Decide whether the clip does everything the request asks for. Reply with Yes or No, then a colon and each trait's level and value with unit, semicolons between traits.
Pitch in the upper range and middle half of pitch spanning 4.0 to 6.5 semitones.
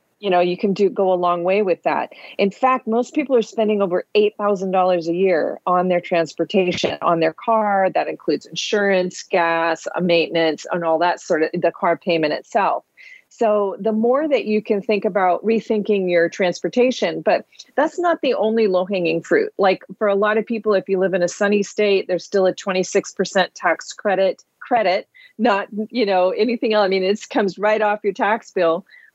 No: high, 195 Hz; average, 3.2 semitones